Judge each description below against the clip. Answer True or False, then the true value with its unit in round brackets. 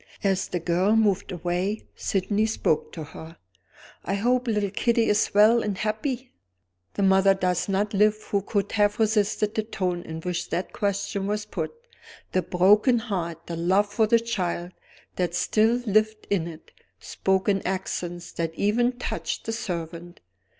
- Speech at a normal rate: True (160 wpm)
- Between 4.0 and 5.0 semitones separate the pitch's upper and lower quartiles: False (3.2 semitones)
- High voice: True (200 Hz)